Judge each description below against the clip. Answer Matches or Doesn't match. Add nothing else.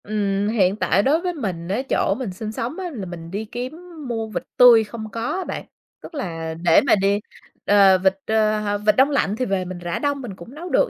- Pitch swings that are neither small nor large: Matches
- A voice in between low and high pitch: Doesn't match